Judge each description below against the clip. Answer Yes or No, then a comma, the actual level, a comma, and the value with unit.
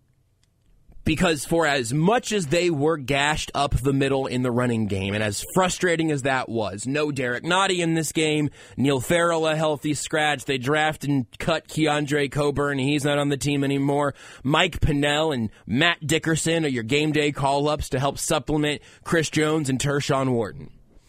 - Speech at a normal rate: Yes, average, 180 wpm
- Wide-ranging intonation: No, average, 2.7 semitones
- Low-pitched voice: No, medium, 145 Hz